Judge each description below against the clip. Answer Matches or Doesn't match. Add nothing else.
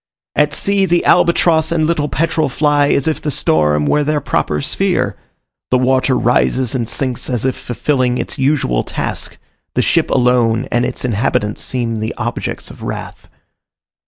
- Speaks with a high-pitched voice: Doesn't match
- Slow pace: Doesn't match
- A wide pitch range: Doesn't match